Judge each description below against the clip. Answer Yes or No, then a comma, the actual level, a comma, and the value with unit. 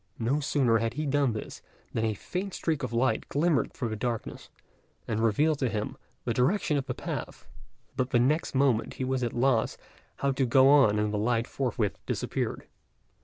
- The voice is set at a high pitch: No, low, 125 Hz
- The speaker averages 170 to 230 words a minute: Yes, average, 195 wpm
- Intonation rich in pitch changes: No, average, 3.7 semitones